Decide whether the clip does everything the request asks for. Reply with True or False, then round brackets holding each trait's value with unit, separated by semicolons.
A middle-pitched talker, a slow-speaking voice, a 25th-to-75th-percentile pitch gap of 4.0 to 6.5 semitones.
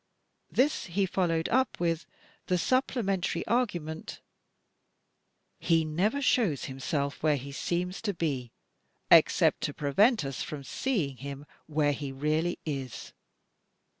True (165 Hz; 120 wpm; 5.6 semitones)